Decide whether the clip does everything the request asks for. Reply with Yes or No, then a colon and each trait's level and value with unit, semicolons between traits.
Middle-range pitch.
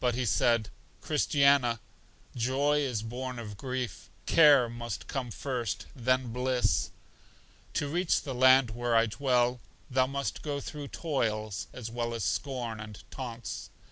No: low, 125 Hz